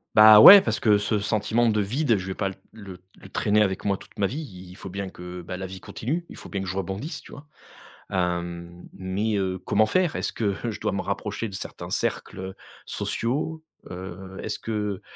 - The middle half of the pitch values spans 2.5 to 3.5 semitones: Yes, average, 2.9 semitones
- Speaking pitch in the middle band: No, low, 100 Hz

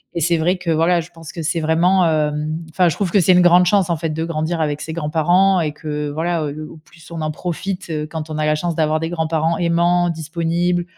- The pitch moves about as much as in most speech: No, narrow, 2.1 semitones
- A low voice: No, medium, 165 Hz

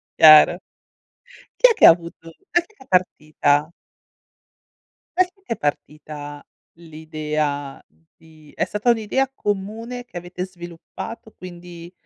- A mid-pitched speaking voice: Yes, medium, 175 Hz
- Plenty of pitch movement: Yes, wide, 6.1 semitones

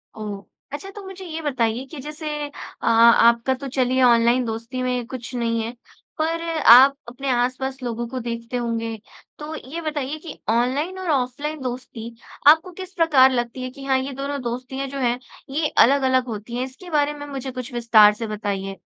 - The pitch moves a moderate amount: Yes, average, 3.6 semitones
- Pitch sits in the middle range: No, very high, 255 Hz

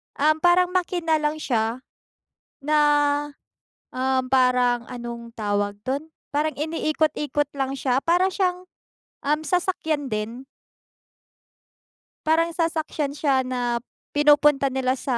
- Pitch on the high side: Yes, very high, 290 Hz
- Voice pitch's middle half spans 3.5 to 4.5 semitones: Yes, average, 3.9 semitones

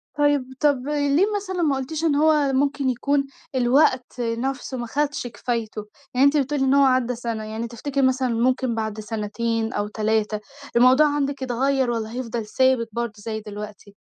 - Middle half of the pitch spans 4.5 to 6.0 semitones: No, average, 3.6 semitones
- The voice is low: No, very high, 255 Hz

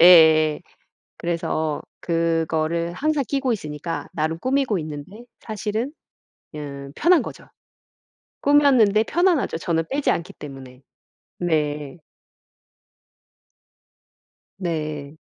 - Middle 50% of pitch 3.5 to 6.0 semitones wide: No, wide, 6.7 semitones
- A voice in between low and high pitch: Yes, medium, 170 Hz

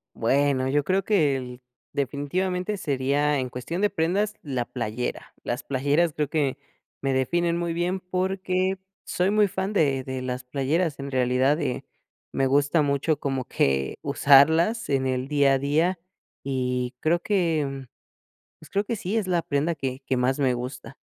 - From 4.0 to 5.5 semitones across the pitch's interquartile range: Yes, average, 4.8 semitones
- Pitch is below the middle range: No, medium, 145 Hz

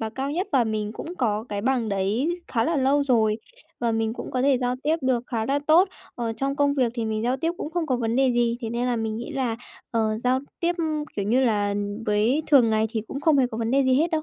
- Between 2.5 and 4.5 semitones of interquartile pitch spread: Yes, average, 3.7 semitones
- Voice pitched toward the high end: Yes, high, 245 Hz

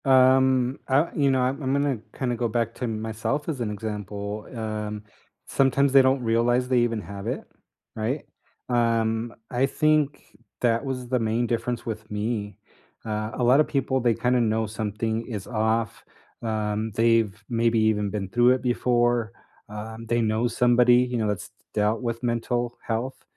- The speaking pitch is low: Yes, low, 115 Hz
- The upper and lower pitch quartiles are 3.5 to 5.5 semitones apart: No, narrow, 2.4 semitones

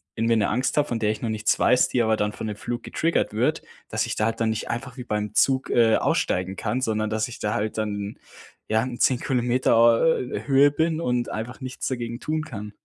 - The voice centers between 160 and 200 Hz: No, low, 115 Hz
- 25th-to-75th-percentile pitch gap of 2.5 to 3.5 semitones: Yes, average, 2.8 semitones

